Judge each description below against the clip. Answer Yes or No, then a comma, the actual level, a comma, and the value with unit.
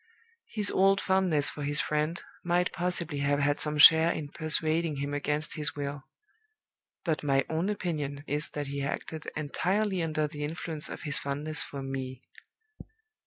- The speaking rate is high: No, average, 160 wpm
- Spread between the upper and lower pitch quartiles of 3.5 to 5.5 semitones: No, narrow, 2.6 semitones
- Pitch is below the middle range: No, medium, 150 Hz